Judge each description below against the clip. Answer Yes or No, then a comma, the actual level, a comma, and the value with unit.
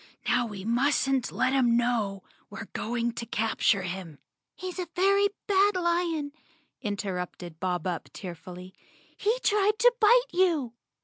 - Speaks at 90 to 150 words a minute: Yes, average, 145 wpm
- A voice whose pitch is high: Yes, high, 240 Hz